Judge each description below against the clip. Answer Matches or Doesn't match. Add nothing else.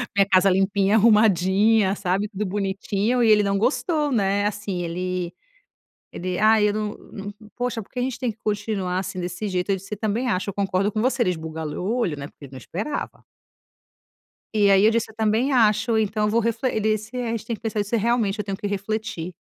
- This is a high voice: Matches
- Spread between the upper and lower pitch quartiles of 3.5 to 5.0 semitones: Doesn't match